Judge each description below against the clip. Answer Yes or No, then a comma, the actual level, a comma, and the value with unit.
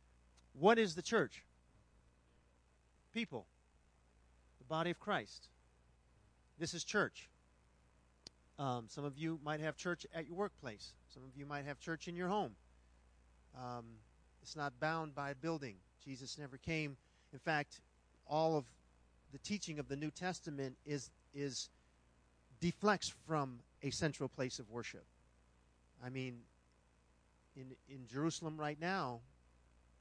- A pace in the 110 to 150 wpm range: Yes, slow, 135 wpm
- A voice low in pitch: Yes, low, 130 Hz